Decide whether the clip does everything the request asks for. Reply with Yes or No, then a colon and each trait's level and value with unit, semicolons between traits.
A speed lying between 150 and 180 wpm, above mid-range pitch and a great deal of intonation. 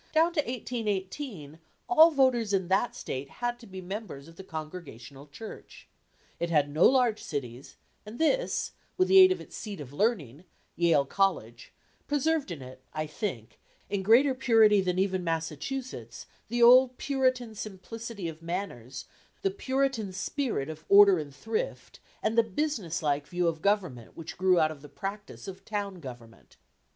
Yes: average, 165 wpm; high, 195 Hz; wide, 7.4 semitones